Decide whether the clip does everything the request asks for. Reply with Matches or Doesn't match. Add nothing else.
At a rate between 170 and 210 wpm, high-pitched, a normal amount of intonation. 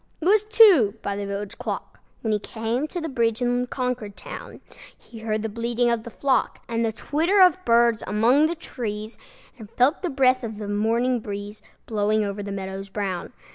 Matches